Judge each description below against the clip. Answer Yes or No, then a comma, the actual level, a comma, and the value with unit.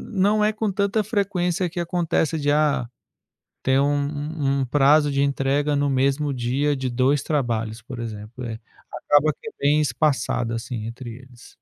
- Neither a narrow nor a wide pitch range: Yes, average, 3.5 semitones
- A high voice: No, medium, 140 Hz